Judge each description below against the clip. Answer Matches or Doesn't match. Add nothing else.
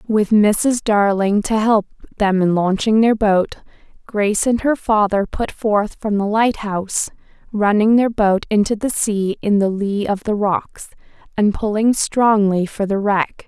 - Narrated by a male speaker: Doesn't match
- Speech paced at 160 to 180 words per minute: Matches